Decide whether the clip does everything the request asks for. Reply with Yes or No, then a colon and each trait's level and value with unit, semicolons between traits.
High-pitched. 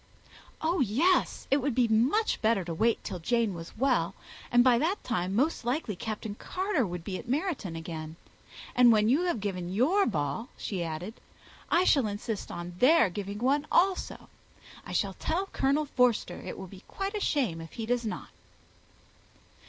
Yes: high, 230 Hz